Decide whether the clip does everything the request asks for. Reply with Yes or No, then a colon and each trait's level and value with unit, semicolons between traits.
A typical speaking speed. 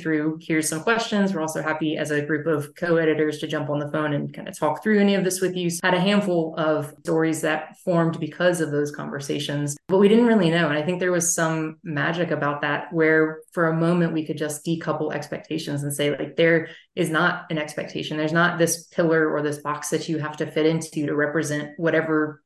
No: fast, 230 wpm